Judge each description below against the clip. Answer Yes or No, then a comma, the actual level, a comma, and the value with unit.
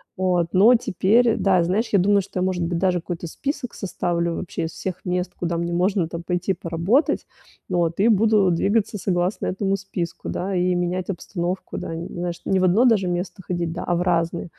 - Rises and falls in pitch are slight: Yes, narrow, 2.2 semitones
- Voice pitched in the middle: Yes, medium, 180 Hz